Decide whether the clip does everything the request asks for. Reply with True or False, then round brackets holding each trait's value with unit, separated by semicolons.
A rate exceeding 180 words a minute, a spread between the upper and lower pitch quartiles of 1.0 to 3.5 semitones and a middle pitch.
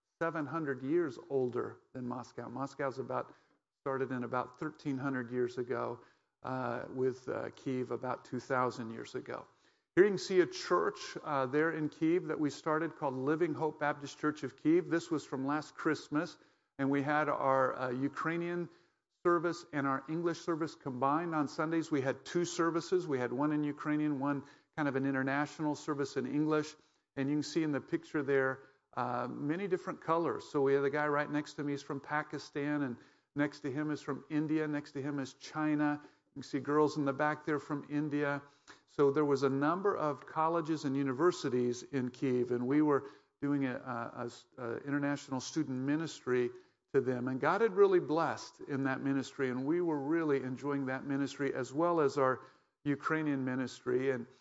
True (190 wpm; 2.5 semitones; 145 Hz)